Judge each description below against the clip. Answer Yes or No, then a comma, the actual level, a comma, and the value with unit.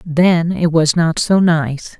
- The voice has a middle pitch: Yes, medium, 165 Hz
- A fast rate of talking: No, average, 180 wpm